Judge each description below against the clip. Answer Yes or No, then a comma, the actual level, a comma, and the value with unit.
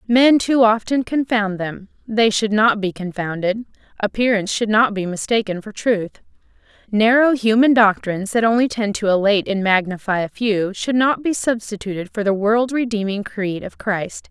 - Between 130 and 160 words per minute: No, average, 170 wpm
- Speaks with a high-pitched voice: Yes, high, 215 Hz